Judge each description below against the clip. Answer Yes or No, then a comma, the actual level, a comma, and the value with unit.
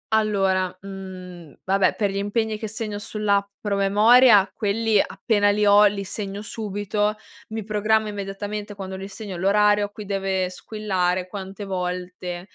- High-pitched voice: Yes, high, 200 Hz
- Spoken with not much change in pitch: Yes, narrow, 1.7 semitones